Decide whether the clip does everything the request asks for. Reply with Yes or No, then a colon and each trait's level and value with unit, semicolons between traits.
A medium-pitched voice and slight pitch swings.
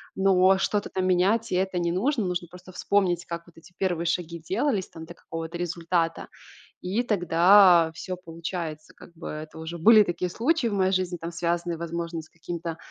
Yes: medium, 175 Hz; narrow, 2.1 semitones